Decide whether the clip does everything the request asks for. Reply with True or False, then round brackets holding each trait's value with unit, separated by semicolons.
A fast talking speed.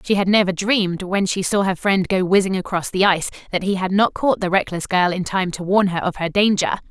True (260 wpm)